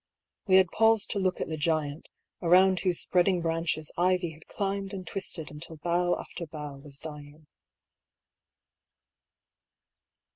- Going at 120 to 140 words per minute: Yes, slow, 135 wpm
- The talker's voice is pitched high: No, medium, 170 Hz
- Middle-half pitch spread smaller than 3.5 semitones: Yes, average, 3.1 semitones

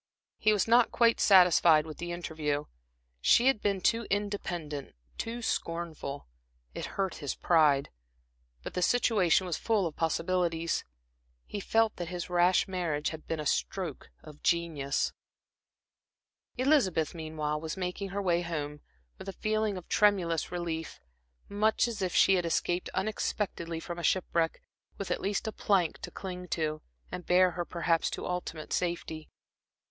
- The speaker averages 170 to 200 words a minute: No, average, 150 wpm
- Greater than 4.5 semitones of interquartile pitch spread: No, average, 3.5 semitones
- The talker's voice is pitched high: No, medium, 175 Hz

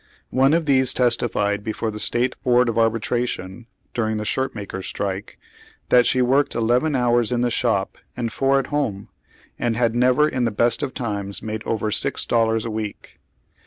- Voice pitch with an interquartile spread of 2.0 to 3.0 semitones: Yes, narrow, 2.6 semitones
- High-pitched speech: No, low, 120 Hz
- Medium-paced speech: Yes, average, 180 wpm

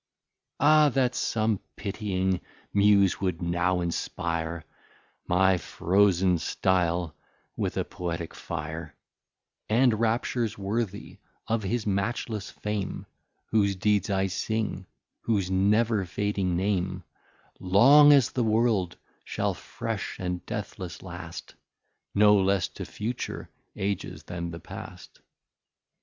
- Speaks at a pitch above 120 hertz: No, very low, 95 Hz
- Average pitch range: Yes, average, 3.3 semitones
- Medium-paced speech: No, slow, 110 wpm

